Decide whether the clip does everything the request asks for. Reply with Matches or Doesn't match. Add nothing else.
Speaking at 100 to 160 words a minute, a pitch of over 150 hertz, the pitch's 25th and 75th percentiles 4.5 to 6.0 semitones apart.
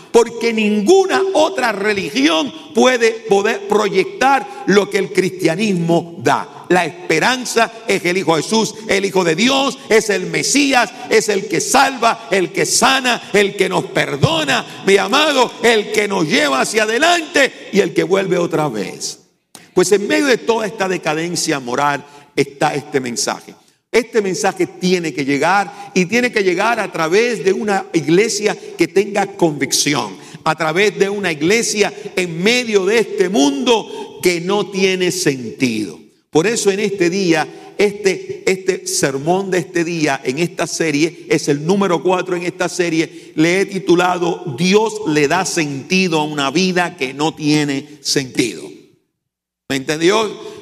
Matches